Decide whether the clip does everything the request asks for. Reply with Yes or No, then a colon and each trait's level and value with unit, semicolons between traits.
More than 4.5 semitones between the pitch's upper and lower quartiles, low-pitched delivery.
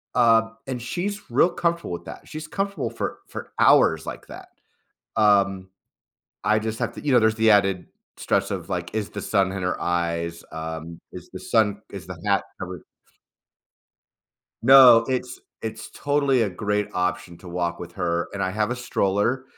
Yes: average, 5.2 semitones; low, 105 Hz